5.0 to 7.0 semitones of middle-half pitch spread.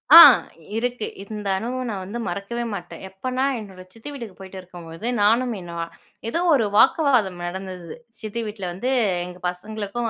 No: average, 4.3 semitones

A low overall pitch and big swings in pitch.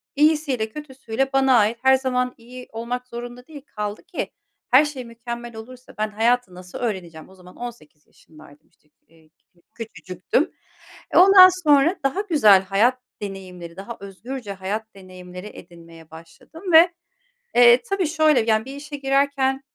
No: high, 240 Hz; wide, 5.7 semitones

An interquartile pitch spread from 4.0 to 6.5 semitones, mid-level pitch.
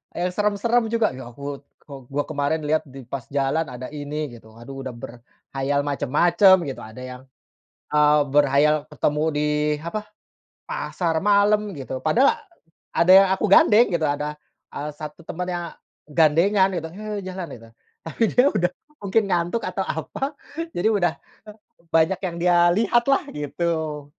Yes: average, 5.0 semitones; medium, 160 Hz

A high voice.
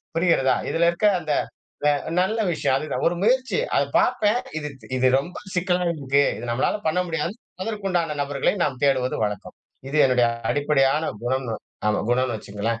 No: medium, 150 Hz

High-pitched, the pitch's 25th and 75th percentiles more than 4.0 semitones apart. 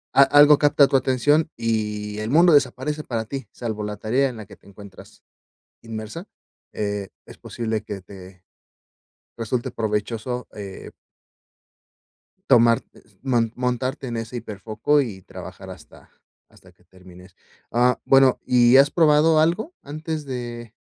No: low, 120 Hz; average, 4.5 semitones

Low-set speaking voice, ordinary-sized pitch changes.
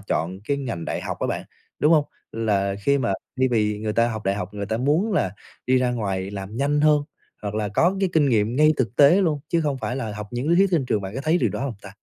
No: low, 120 Hz; wide, 6.0 semitones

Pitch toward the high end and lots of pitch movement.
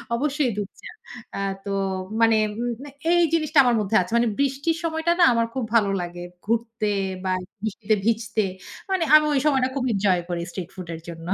Yes: high, 230 Hz; wide, 6.0 semitones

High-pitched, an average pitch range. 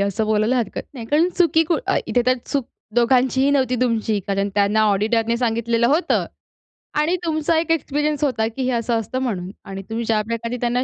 Yes: high, 235 Hz; average, 3.7 semitones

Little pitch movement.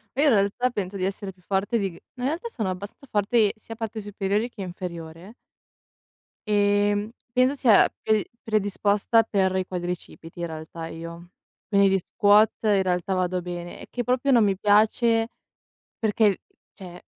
No: average, 3.2 semitones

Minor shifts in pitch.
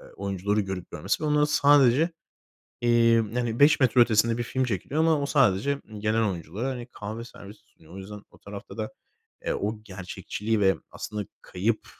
No: average, 4.0 semitones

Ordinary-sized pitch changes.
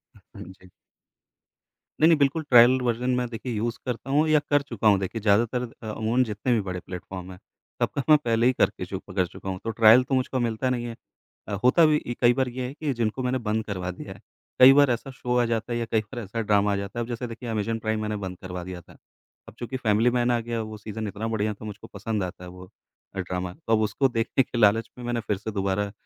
Yes: average, 3.4 semitones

